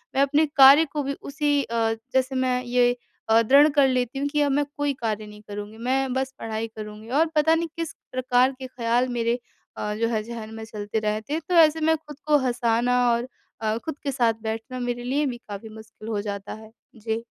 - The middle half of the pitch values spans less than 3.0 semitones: No, average, 4.0 semitones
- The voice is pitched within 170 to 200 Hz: No, high, 245 Hz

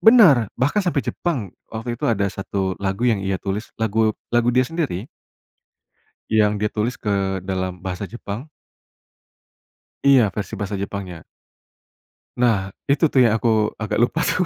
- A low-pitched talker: Yes, low, 110 Hz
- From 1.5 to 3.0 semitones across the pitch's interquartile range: No, average, 4.1 semitones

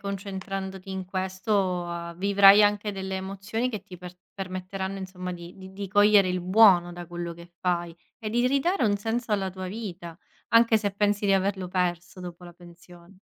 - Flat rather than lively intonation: Yes, narrow, 2.3 semitones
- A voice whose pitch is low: No, high, 190 Hz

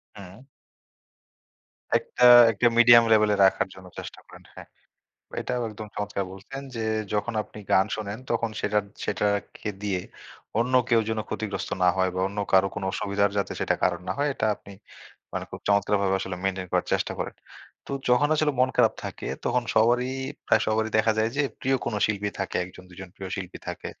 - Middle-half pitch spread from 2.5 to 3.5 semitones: Yes, average, 3.2 semitones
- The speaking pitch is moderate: No, low, 105 Hz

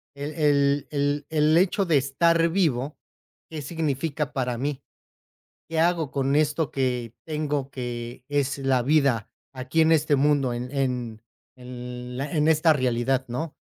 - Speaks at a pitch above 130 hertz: Yes, medium, 140 Hz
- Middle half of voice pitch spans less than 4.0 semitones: Yes, average, 3.4 semitones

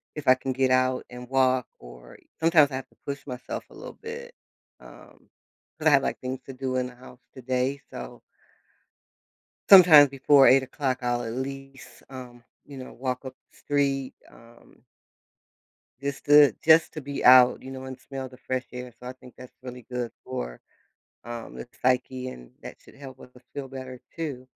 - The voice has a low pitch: Yes, low, 130 Hz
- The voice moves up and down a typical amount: No, narrow, 1.6 semitones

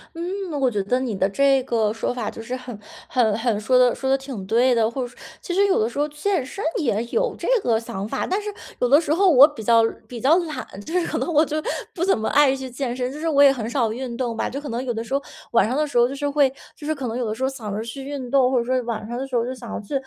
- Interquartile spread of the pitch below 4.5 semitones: Yes, average, 3.7 semitones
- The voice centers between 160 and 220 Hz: No, very high, 255 Hz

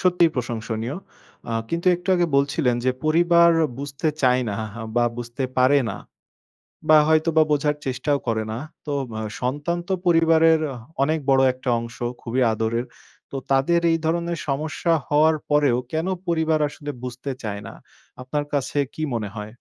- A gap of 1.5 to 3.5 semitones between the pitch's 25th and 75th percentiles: No, average, 4.3 semitones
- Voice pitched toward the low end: No, medium, 145 Hz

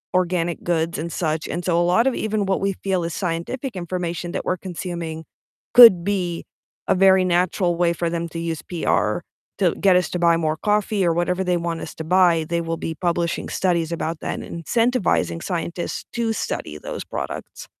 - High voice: No, medium, 175 Hz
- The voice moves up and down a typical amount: No, narrow, 2.0 semitones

